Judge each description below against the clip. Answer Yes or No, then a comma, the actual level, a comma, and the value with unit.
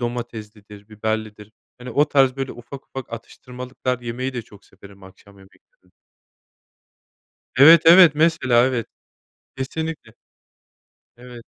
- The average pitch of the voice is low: Yes, low, 120 Hz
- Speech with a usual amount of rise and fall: Yes, average, 3.7 semitones